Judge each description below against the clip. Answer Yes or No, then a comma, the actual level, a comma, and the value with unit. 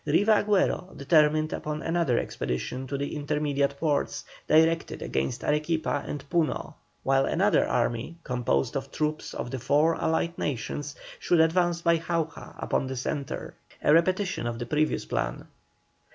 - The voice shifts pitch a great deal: No, average, 3.3 semitones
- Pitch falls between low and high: Yes, medium, 150 Hz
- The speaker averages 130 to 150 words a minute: Yes, average, 145 wpm